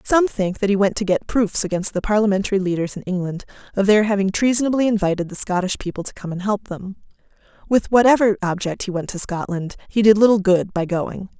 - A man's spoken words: No, female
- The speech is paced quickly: Yes, fast, 210 wpm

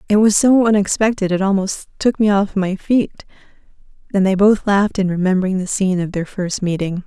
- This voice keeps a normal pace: Yes, average, 195 wpm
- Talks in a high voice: Yes, high, 195 Hz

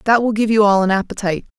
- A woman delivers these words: Yes, female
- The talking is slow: No, fast, 265 wpm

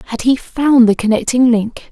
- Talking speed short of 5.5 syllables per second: Yes, 4.9 syllables/s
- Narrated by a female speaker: Yes, female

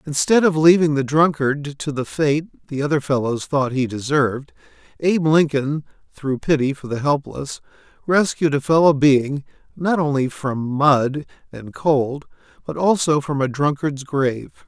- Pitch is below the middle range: No, medium, 145 Hz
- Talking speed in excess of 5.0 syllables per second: No, 4.4 syllables/s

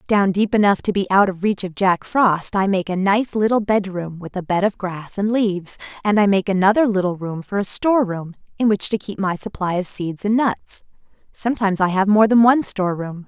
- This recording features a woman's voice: Yes, female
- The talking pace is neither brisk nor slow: No, fast, 225 wpm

